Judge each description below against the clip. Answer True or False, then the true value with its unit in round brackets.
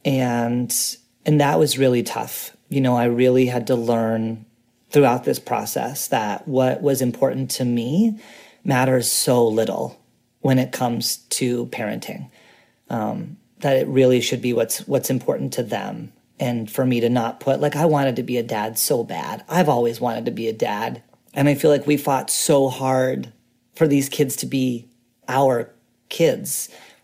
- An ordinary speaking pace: True (175 wpm)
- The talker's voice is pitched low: True (125 Hz)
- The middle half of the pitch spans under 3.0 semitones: True (2.4 semitones)